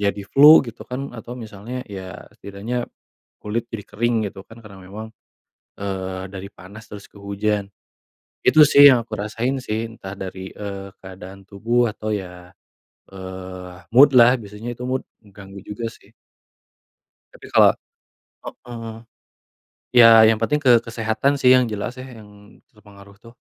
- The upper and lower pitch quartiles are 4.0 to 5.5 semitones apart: No, average, 3.2 semitones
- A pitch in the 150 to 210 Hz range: No, low, 105 Hz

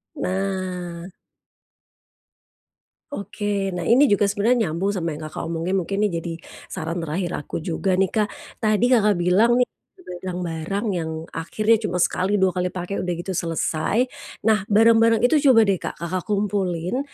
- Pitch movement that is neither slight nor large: Yes, average, 3.4 semitones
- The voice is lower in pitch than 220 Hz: Yes, high, 190 Hz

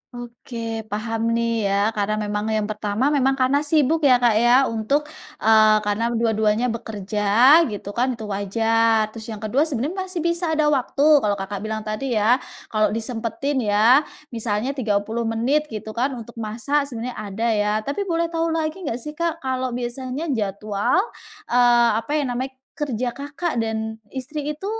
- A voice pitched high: Yes, high, 230 Hz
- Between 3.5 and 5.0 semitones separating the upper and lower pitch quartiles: Yes, average, 3.9 semitones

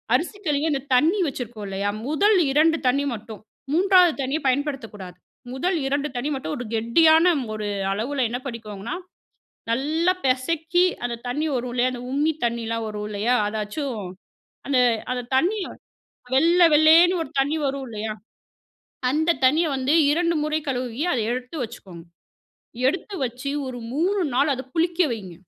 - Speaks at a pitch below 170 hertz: No, very high, 265 Hz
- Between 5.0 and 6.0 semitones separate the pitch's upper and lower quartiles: Yes, wide, 5.4 semitones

